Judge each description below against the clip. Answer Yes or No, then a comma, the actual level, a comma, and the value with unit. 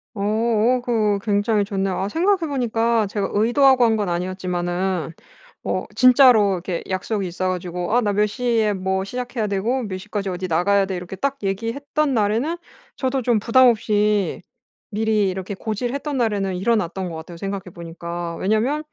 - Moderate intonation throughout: Yes, average, 4.0 semitones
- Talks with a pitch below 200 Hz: No, high, 205 Hz